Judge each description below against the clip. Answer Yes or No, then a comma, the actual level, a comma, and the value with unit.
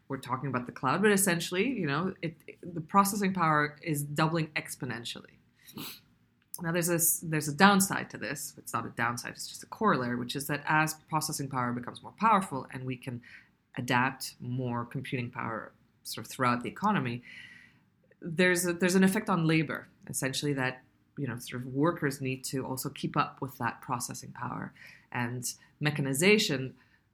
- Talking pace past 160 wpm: Yes, average, 175 wpm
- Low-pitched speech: No, medium, 145 Hz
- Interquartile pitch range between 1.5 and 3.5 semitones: No, average, 4.8 semitones